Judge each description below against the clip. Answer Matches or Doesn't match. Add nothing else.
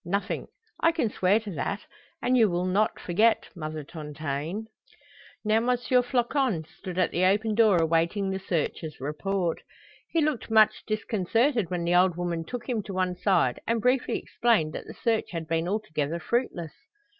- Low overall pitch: Doesn't match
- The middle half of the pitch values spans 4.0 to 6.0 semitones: Matches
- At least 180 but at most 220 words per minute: Doesn't match